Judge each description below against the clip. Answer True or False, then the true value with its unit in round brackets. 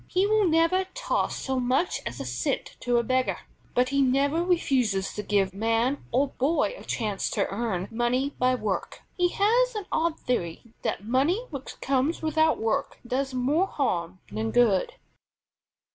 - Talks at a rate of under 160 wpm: False (165 wpm)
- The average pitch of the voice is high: True (260 Hz)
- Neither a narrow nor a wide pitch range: False (6.3 semitones)